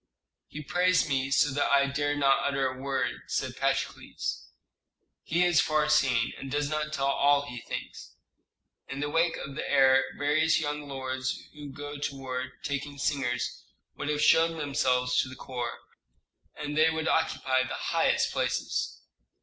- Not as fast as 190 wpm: Yes, average, 165 wpm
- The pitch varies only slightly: Yes, narrow, 2.2 semitones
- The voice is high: No, medium, 140 Hz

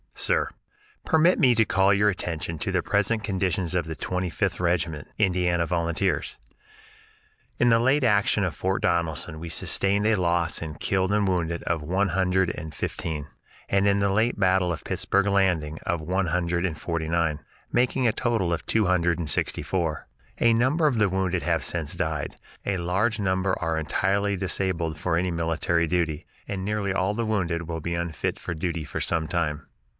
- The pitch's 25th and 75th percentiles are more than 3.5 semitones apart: No, average, 3.1 semitones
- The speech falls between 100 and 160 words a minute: No, average, 185 wpm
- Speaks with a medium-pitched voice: No, very low, 90 Hz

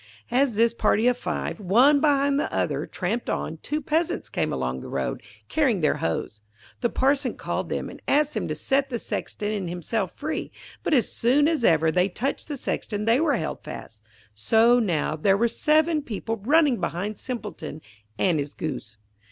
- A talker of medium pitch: No, high, 230 Hz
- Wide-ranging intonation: Yes, wide, 7.9 semitones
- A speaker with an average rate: Yes, average, 185 wpm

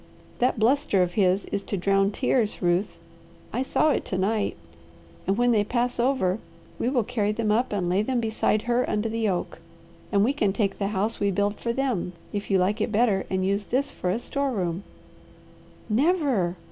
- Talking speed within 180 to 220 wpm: Yes, average, 195 wpm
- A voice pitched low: No, high, 210 Hz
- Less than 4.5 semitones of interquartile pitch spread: Yes, average, 3.7 semitones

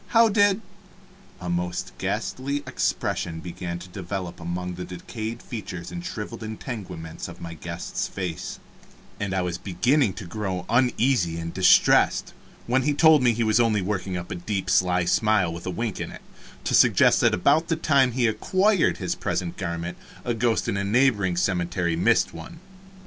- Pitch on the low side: Yes, low, 100 Hz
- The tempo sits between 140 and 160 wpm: No, average, 175 wpm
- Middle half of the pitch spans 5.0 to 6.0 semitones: Yes, wide, 5.5 semitones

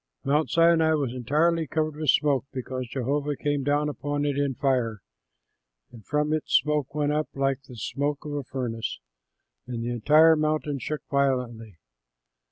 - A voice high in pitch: No, medium, 145 Hz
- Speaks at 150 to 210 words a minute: Yes, average, 160 wpm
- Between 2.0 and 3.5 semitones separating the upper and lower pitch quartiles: Yes, average, 2.7 semitones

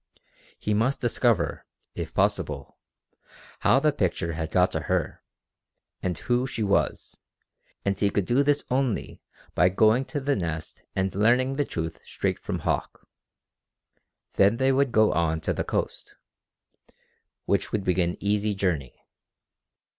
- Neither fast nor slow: Yes, average, 145 wpm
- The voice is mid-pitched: No, low, 105 Hz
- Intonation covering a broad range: Yes, wide, 6.0 semitones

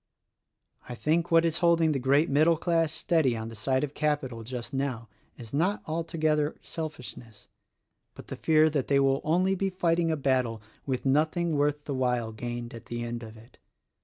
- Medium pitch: Yes, medium, 145 Hz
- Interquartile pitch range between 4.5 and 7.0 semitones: Yes, average, 4.9 semitones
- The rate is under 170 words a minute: No, average, 185 wpm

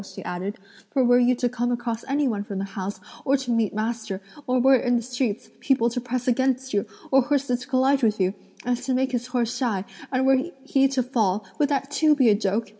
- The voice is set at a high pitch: Yes, high, 245 Hz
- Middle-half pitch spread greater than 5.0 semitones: No, average, 3.0 semitones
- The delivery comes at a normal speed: No, fast, 235 wpm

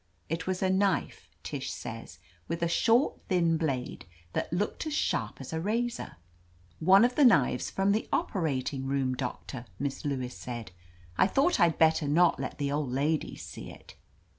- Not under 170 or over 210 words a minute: Yes, average, 175 wpm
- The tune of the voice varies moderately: No, wide, 5.9 semitones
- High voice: No, medium, 165 Hz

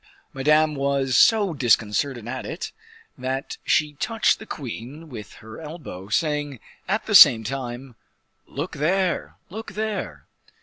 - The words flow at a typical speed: No, slow, 130 wpm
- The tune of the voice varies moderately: Yes, average, 4.5 semitones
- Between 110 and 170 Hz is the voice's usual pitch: Yes, medium, 140 Hz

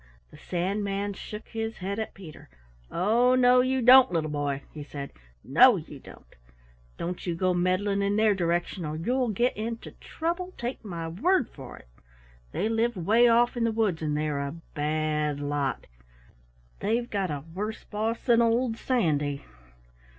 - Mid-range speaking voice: No, high, 200 Hz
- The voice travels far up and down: Yes, wide, 6.8 semitones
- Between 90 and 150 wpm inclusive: No, average, 165 wpm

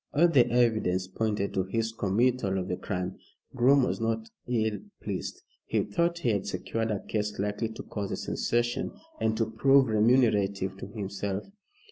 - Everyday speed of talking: Yes, average, 165 wpm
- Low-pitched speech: Yes, low, 110 Hz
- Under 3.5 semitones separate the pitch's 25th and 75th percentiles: Yes, average, 3.0 semitones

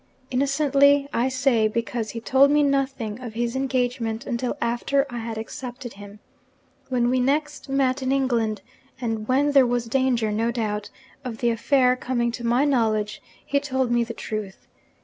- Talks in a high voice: Yes, high, 245 Hz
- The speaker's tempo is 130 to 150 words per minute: No, average, 170 wpm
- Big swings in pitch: No, average, 2.9 semitones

